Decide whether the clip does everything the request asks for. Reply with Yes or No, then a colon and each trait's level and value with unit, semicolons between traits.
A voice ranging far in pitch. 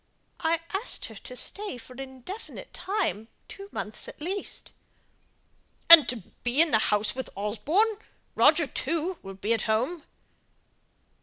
Yes: wide, 8.1 semitones